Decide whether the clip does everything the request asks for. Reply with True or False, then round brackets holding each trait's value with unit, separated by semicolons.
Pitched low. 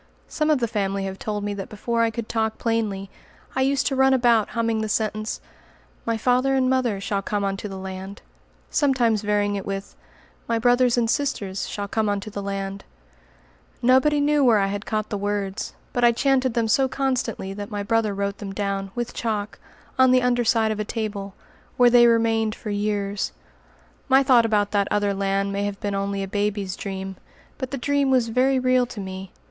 False (215 Hz)